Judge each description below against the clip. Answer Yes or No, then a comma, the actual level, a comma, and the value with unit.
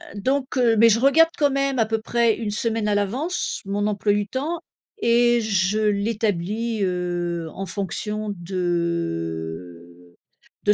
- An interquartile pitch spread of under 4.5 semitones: No, average, 4.8 semitones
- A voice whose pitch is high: Yes, high, 210 Hz